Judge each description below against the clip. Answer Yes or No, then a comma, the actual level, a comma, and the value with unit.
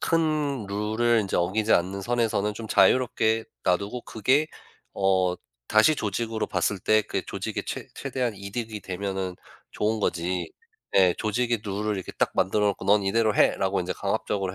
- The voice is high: No, low, 105 Hz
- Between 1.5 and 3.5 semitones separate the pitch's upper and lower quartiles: Yes, average, 2.9 semitones